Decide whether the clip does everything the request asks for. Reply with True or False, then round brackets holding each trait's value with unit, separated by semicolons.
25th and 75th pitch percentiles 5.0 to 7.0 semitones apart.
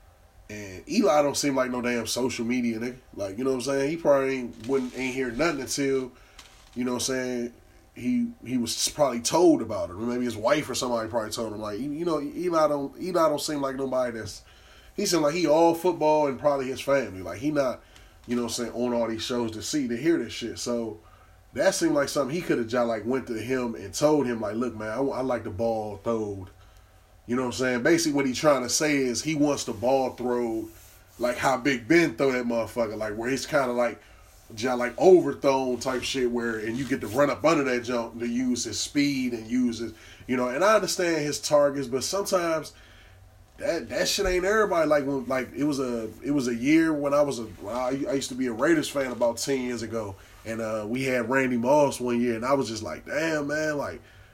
False (3.9 semitones)